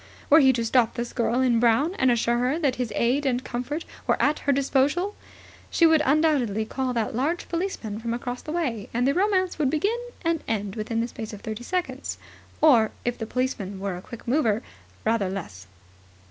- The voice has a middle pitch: No, very high, 250 Hz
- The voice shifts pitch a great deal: No, average, 4.9 semitones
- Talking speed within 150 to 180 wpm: No, average, 200 wpm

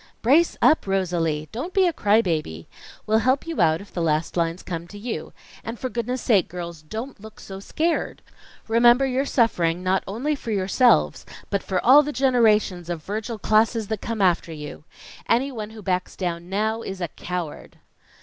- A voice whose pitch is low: No, high, 210 Hz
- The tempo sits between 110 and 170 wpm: No, average, 180 wpm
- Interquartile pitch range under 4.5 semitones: No, wide, 5.4 semitones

